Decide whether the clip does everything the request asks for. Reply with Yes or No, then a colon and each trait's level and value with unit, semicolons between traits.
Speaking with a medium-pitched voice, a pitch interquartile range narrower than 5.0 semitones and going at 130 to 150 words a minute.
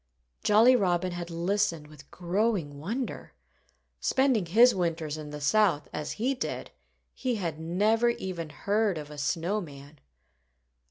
No: medium, 175 Hz; wide, 5.6 semitones; average, 140 wpm